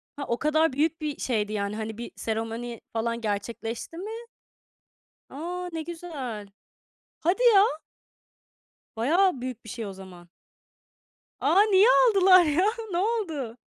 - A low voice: No, very high, 270 Hz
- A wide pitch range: Yes, wide, 7.6 semitones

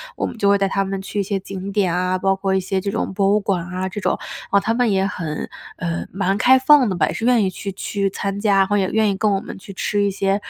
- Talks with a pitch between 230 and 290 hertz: No, high, 195 Hz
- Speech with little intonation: Yes, narrow, 1.3 semitones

